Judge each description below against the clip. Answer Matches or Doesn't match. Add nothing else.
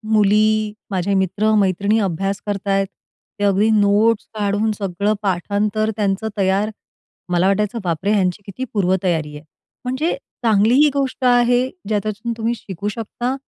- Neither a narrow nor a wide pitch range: Doesn't match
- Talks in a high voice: Matches